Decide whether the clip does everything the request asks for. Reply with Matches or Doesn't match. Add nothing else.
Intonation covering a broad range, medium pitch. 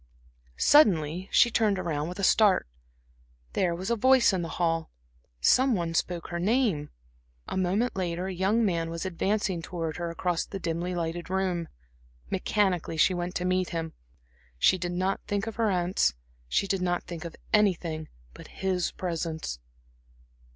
Doesn't match